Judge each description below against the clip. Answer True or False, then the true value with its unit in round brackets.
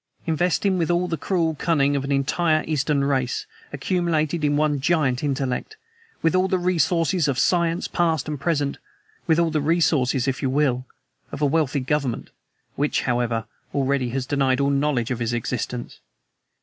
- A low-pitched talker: False (145 Hz)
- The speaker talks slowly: False (170 wpm)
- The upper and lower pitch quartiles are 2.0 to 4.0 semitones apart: True (3.7 semitones)